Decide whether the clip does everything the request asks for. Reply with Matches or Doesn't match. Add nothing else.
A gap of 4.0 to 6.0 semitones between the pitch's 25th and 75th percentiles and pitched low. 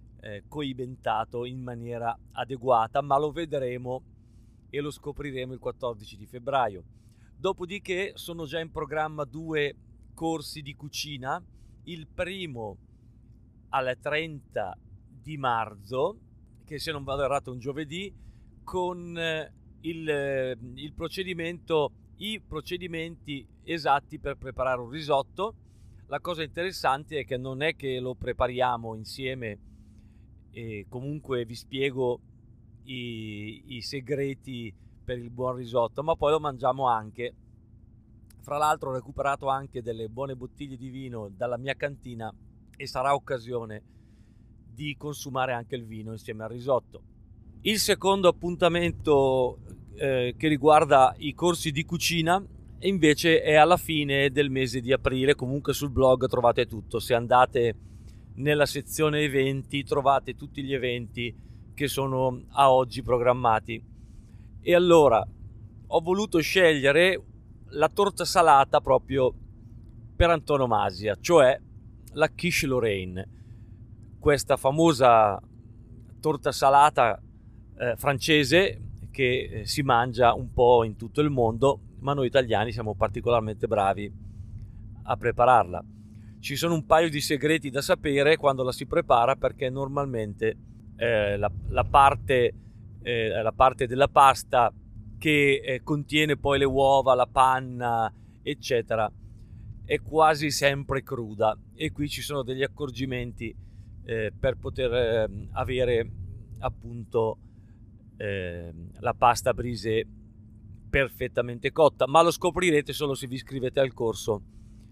Matches